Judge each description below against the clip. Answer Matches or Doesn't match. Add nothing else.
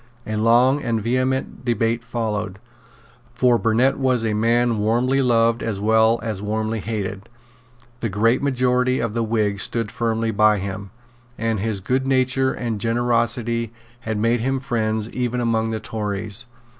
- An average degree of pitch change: Doesn't match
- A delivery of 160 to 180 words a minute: Doesn't match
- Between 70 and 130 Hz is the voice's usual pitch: Matches